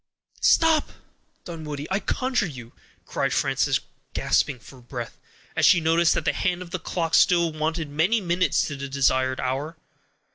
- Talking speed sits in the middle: Yes, average, 155 wpm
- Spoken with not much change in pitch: No, average, 4.2 semitones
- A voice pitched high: No, medium, 160 Hz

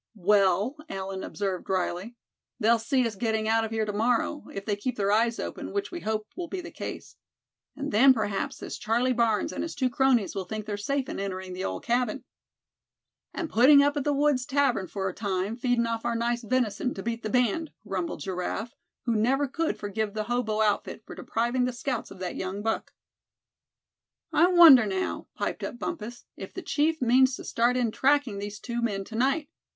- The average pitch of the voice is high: Yes, high, 230 Hz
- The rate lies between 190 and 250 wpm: Yes, average, 200 wpm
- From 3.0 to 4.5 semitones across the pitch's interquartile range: Yes, average, 4.0 semitones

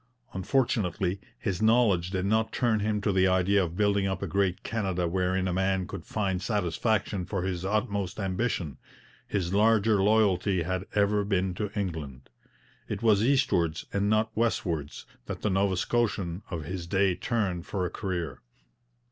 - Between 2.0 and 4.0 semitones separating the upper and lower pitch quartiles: Yes, average, 2.7 semitones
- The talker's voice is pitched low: Yes, very low, 95 Hz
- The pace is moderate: Yes, average, 160 wpm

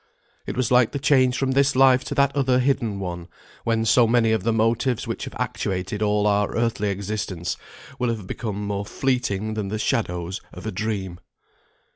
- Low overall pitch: Yes, low, 110 Hz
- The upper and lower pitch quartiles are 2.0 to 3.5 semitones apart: No, average, 3.9 semitones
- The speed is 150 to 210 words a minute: Yes, average, 185 wpm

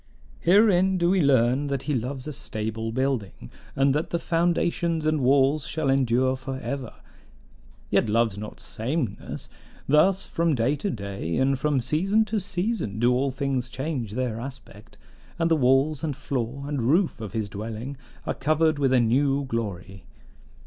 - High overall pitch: No, low, 135 Hz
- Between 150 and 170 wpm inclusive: Yes, average, 165 wpm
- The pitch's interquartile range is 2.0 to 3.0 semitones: No, average, 4.8 semitones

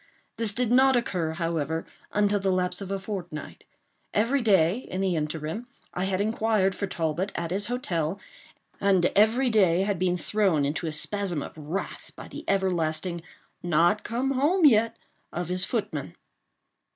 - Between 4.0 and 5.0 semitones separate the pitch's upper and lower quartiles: Yes, average, 4.3 semitones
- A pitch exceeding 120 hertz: Yes, high, 190 Hz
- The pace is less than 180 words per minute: Yes, average, 160 wpm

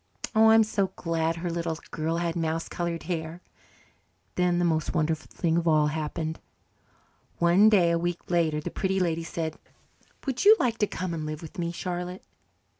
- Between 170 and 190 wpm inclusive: Yes, average, 180 wpm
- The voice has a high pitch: No, medium, 170 Hz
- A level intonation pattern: Yes, narrow, 1.9 semitones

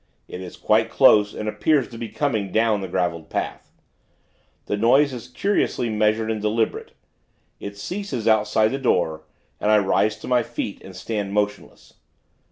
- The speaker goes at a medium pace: Yes, average, 165 wpm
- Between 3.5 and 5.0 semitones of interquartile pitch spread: No, narrow, 2.5 semitones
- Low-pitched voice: Yes, low, 110 Hz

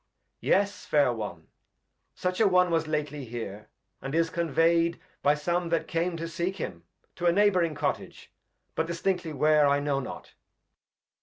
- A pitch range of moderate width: Yes, average, 3.3 semitones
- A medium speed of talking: Yes, average, 155 wpm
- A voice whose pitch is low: No, medium, 165 Hz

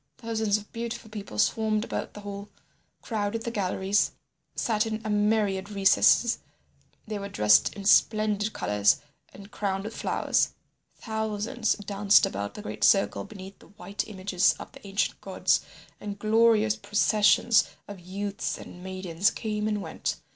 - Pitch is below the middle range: No, high, 205 Hz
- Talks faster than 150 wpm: No, average, 145 wpm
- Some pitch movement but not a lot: No, narrow, 1.8 semitones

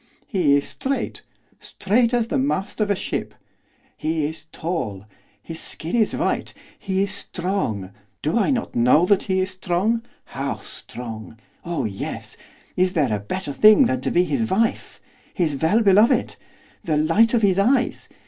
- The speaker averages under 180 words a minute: Yes, average, 165 wpm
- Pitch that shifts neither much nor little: No, wide, 5.9 semitones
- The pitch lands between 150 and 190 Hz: Yes, medium, 185 Hz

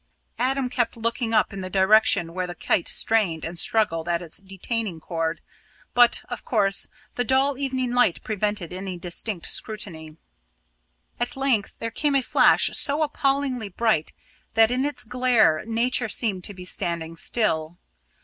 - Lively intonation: Yes, wide, 5.7 semitones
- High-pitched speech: Yes, high, 215 Hz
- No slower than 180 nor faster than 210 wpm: No, average, 155 wpm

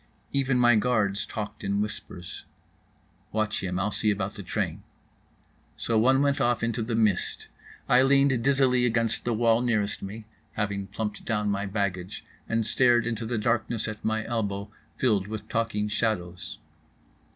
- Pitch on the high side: No, low, 110 Hz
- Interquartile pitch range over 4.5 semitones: No, average, 2.8 semitones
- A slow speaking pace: No, average, 155 wpm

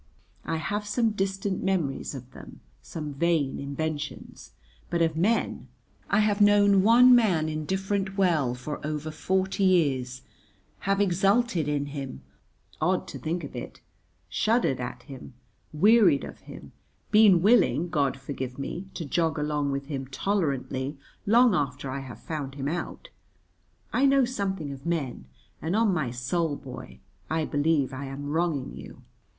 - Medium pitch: Yes, medium, 160 Hz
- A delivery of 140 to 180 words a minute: Yes, average, 150 wpm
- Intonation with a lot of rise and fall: Yes, wide, 5.9 semitones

